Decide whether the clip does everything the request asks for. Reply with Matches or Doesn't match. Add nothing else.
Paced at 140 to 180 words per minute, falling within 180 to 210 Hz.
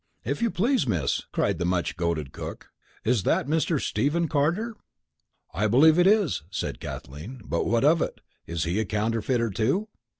Doesn't match